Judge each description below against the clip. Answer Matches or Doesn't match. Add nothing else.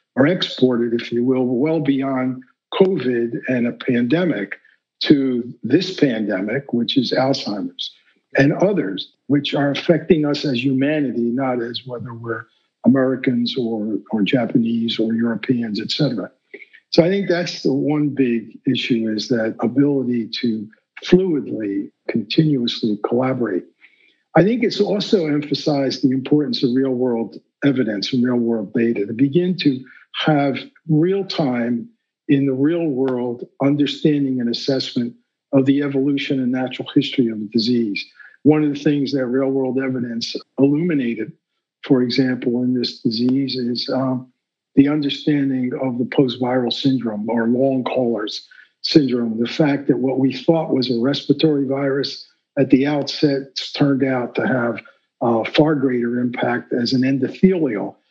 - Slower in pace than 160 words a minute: Matches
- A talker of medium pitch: Doesn't match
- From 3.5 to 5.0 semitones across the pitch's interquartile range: Doesn't match